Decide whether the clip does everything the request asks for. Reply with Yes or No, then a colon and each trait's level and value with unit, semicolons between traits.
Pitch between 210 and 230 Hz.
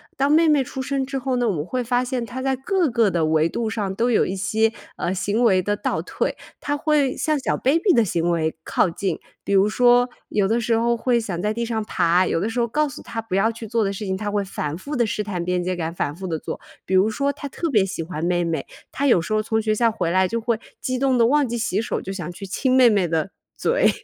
Yes: high, 220 Hz